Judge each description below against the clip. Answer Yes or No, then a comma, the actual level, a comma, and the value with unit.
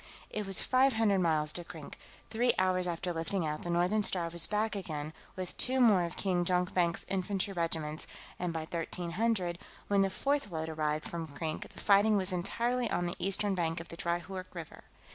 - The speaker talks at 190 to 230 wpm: Yes, average, 195 wpm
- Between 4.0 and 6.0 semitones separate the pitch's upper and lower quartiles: No, average, 3.2 semitones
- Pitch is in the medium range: Yes, medium, 180 Hz